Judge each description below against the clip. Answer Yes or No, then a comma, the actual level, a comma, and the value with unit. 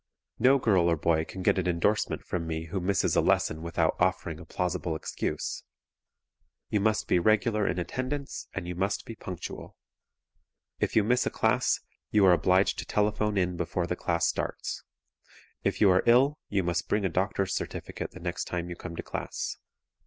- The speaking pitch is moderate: No, very low, 95 Hz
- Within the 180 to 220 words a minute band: Yes, average, 185 wpm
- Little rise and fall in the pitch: No, average, 3.5 semitones